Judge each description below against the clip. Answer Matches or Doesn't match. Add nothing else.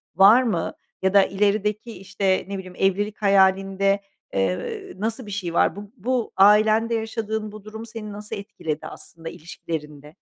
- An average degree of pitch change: Doesn't match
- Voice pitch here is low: Doesn't match